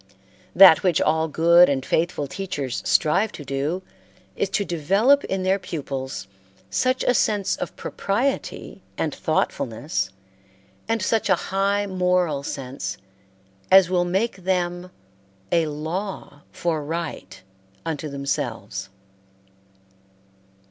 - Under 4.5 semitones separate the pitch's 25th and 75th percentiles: No, average, 5.0 semitones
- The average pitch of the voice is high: No, medium, 175 Hz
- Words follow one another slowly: Yes, slow, 115 wpm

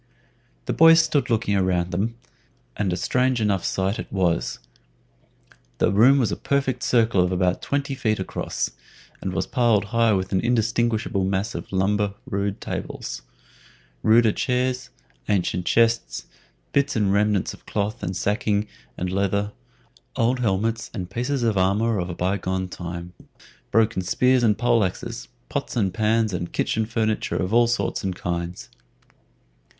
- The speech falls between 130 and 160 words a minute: Yes, average, 155 wpm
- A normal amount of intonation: Yes, average, 3.7 semitones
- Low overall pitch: Yes, low, 105 Hz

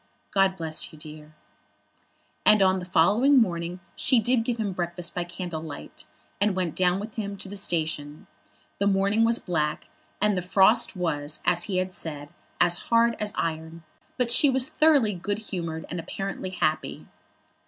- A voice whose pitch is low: No, medium, 185 Hz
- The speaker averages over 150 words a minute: Yes, average, 175 wpm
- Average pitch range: Yes, average, 4.1 semitones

